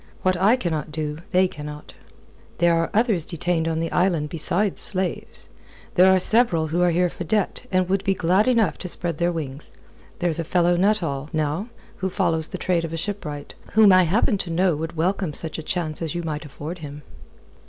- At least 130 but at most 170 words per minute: No, average, 200 wpm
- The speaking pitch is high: No, medium, 175 Hz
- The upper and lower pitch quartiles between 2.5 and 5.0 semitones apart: Yes, average, 2.9 semitones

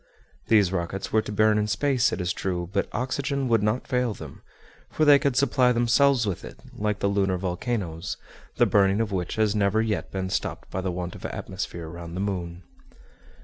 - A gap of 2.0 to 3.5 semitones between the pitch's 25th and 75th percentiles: No, average, 4.5 semitones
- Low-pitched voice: Yes, low, 100 Hz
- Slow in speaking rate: No, average, 195 wpm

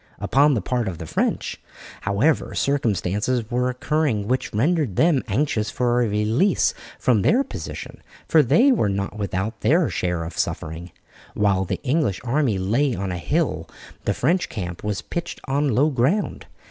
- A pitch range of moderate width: No, wide, 6.4 semitones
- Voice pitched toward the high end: No, low, 120 Hz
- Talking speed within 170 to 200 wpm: No, average, 160 wpm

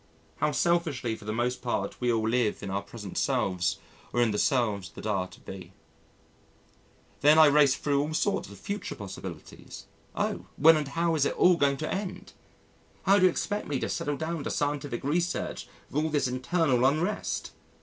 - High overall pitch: No, medium, 140 Hz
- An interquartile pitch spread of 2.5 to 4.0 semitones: No, average, 5.3 semitones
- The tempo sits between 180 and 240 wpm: Yes, average, 190 wpm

